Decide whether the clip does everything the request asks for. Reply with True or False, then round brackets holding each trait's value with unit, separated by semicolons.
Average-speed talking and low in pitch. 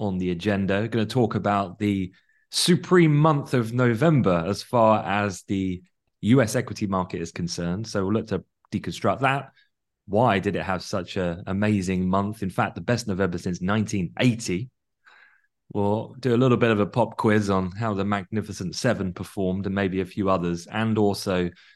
True (180 wpm; 100 Hz)